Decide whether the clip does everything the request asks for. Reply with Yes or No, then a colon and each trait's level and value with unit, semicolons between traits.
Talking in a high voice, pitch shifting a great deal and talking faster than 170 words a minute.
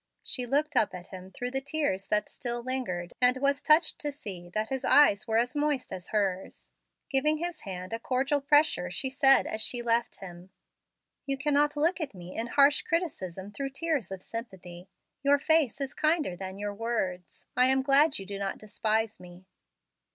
Yes: high, 245 Hz; wide, 6.8 semitones; average, 190 wpm